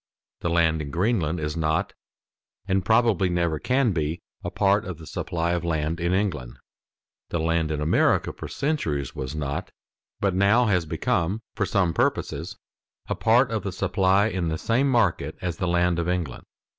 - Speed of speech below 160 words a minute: No, average, 175 wpm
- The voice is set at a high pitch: No, very low, 85 Hz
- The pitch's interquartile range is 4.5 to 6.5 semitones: No, average, 3.8 semitones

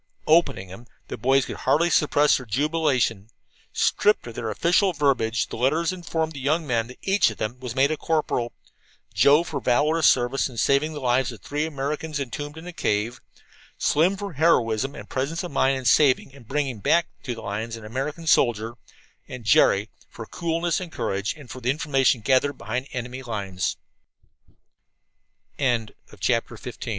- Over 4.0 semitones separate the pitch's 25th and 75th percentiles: Yes, average, 4.7 semitones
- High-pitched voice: No, low, 135 Hz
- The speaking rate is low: No, average, 165 wpm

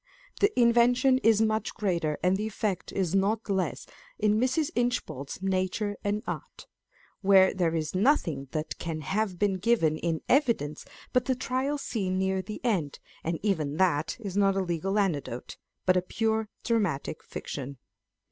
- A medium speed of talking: Yes, average, 155 wpm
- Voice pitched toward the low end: No, high, 195 Hz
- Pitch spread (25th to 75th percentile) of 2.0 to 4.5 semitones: No, average, 5.0 semitones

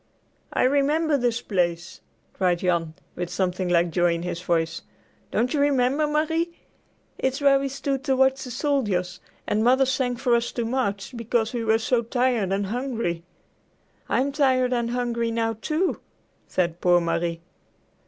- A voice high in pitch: Yes, high, 235 Hz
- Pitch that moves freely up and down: Yes, wide, 6.7 semitones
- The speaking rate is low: No, average, 160 wpm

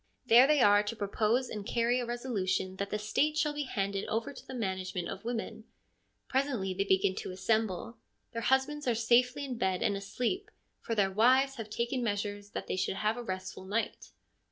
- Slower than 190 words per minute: No, average, 195 wpm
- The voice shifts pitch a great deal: No, average, 4.1 semitones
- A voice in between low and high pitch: No, high, 225 Hz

